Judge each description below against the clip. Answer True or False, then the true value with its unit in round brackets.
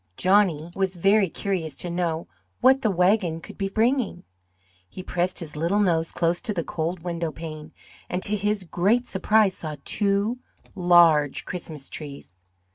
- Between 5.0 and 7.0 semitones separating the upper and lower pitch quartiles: False (3.5 semitones)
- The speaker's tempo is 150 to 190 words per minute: True (155 wpm)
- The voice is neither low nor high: True (180 Hz)